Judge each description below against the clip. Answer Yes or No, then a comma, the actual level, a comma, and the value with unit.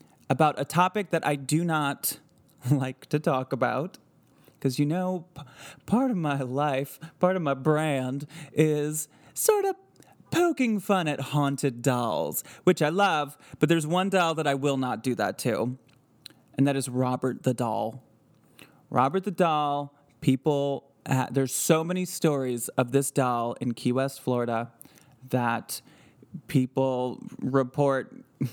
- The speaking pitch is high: No, medium, 140 Hz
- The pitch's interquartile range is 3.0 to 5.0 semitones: Yes, average, 3.4 semitones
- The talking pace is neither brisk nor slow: Yes, average, 145 wpm